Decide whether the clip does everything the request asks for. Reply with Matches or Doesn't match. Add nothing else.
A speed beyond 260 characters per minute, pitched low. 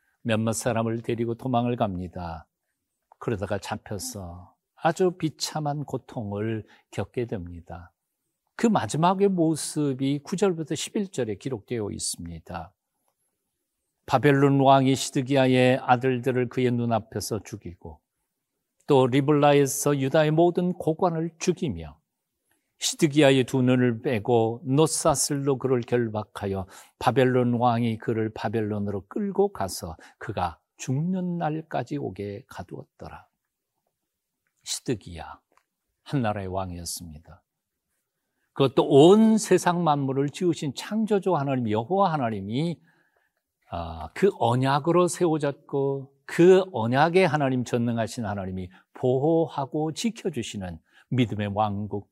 Doesn't match